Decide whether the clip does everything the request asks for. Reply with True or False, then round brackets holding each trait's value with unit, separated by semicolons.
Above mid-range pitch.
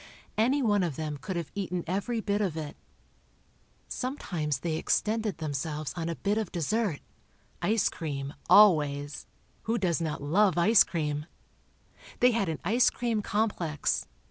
False (175 Hz)